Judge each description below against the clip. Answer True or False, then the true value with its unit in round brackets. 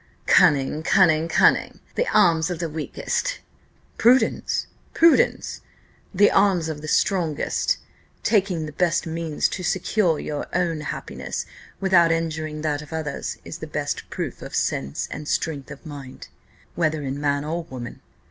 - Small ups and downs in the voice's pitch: False (3.2 semitones)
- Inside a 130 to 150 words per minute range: True (145 wpm)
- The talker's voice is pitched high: False (160 Hz)